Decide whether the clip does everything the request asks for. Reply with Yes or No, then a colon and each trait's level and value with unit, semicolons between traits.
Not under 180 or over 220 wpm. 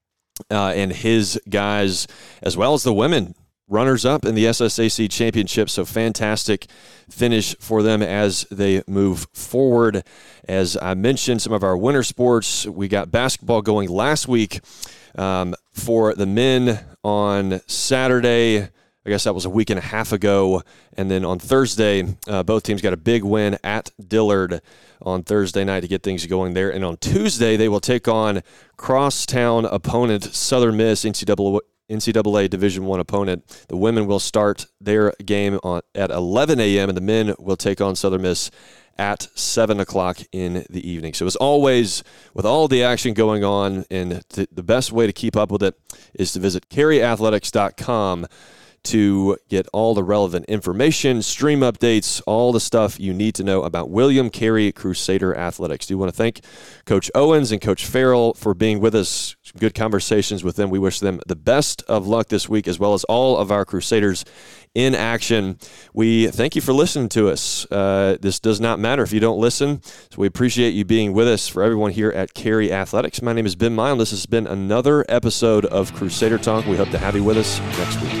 Yes: average, 190 wpm